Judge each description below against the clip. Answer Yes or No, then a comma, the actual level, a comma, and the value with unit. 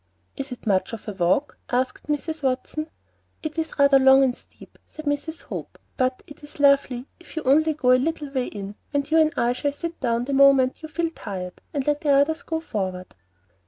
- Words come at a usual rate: No, fast, 215 wpm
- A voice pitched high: Yes, very high, 275 Hz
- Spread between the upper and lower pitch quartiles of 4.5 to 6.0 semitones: No, average, 3.6 semitones